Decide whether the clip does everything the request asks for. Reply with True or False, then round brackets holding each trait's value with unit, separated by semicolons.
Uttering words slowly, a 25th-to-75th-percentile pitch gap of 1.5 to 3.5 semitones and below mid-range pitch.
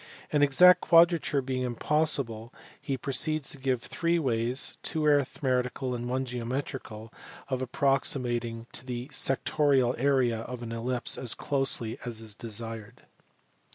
True (130 wpm; 2.9 semitones; 130 Hz)